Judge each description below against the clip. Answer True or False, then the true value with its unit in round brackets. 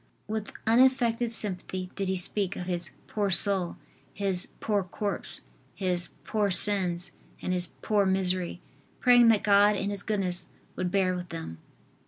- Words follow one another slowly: False (150 wpm)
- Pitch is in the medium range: False (195 Hz)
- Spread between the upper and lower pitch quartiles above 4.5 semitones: False (2.5 semitones)